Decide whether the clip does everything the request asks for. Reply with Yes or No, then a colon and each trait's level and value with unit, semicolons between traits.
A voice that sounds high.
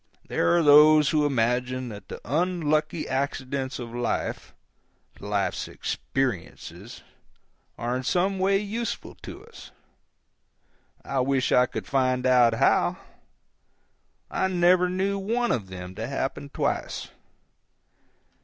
No: low, 135 Hz